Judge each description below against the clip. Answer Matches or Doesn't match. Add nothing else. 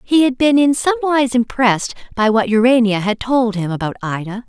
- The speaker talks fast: Doesn't match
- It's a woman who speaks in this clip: Matches